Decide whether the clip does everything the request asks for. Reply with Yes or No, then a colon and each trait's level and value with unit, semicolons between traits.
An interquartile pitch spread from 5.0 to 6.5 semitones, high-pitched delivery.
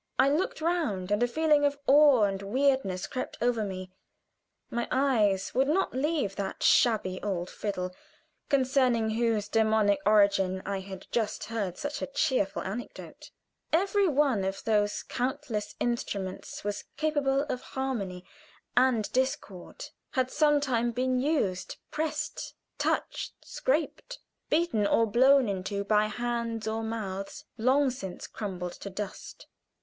Yes: average, 5.3 semitones; high, 230 Hz